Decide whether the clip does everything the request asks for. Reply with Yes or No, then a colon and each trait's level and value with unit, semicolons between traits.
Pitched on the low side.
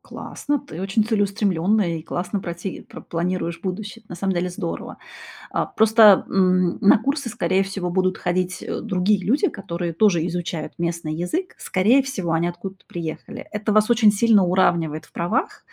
No: medium, 185 Hz